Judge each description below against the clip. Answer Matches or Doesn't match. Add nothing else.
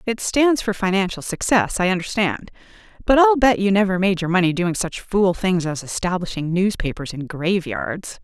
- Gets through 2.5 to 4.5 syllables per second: Doesn't match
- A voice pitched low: Doesn't match